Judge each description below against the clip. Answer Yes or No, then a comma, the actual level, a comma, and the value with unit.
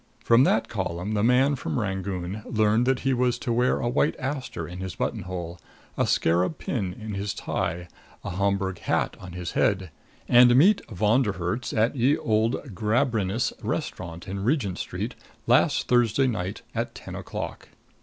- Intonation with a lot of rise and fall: No, average, 4.9 semitones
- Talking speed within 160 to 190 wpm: Yes, average, 170 wpm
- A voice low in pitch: Yes, low, 105 Hz